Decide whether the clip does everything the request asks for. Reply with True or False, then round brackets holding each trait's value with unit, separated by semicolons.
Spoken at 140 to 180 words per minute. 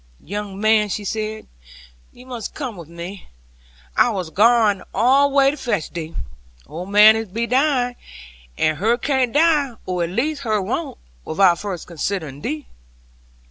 True (155 wpm)